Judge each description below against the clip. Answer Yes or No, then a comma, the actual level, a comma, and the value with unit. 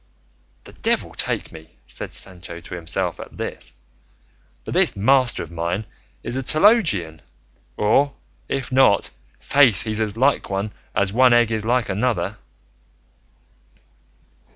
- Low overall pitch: Yes, low, 110 Hz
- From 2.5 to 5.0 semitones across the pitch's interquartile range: No, wide, 5.5 semitones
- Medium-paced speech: No, slow, 130 wpm